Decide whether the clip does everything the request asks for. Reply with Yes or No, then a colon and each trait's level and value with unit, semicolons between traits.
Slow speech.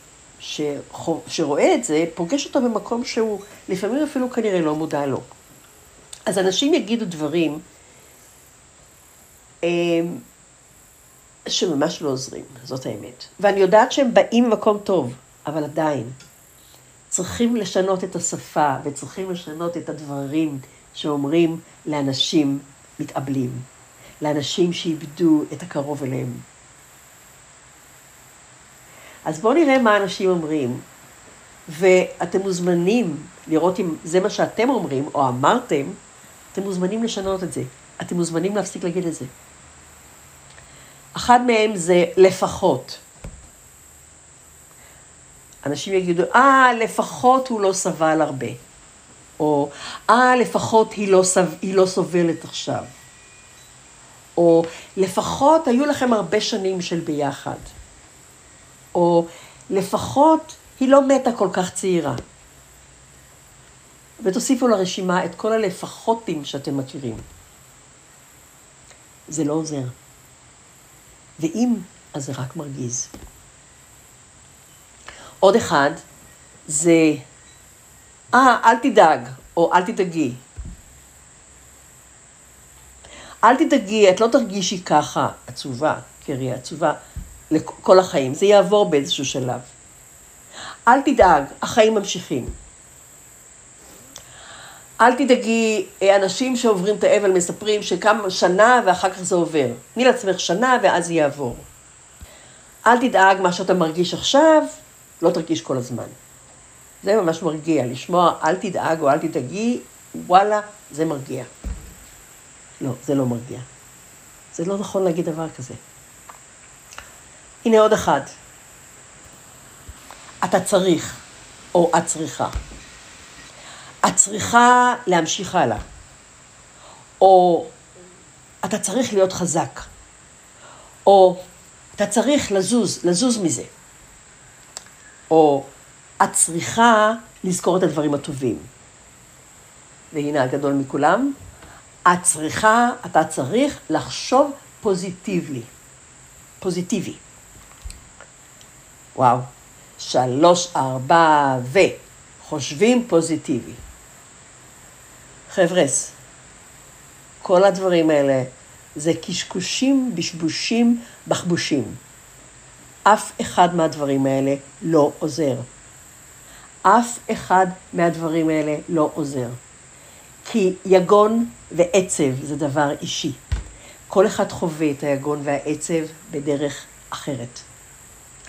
Yes: slow, 95 wpm